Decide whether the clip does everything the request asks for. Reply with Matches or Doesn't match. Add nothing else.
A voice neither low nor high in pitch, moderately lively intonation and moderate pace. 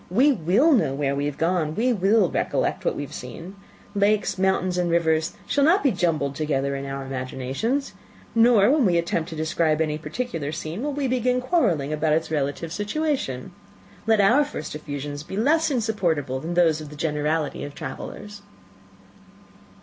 Doesn't match